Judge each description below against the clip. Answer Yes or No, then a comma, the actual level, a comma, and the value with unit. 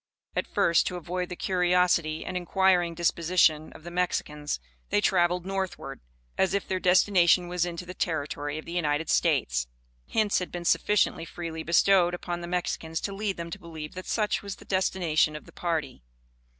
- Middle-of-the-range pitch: Yes, medium, 175 Hz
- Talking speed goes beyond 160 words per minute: Yes, average, 175 wpm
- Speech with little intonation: Yes, narrow, 2.1 semitones